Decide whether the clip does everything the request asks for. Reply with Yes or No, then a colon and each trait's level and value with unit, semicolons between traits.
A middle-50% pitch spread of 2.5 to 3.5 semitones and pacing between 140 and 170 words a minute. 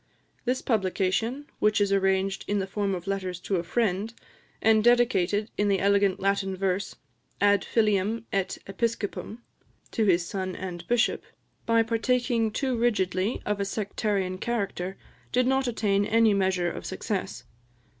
Yes: average, 3.1 semitones; average, 145 wpm